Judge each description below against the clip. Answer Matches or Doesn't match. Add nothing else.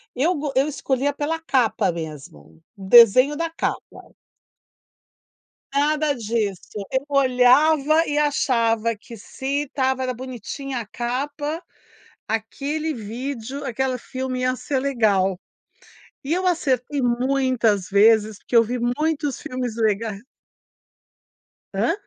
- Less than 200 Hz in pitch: Doesn't match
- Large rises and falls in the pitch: Doesn't match